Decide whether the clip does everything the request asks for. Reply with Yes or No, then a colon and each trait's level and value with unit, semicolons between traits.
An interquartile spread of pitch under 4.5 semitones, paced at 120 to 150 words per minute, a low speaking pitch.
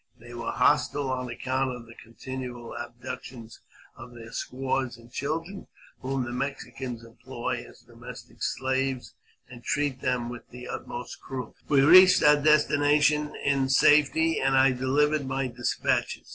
Yes: average, 2.8 semitones; average, 140 wpm; low, 130 Hz